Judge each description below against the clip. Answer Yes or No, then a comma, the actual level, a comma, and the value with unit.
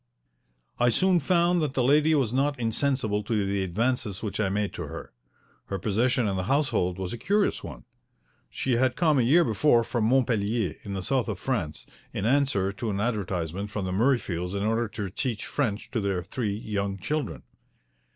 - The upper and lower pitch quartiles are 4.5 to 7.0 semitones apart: Yes, average, 4.9 semitones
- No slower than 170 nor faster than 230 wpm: Yes, average, 190 wpm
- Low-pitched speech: Yes, low, 110 Hz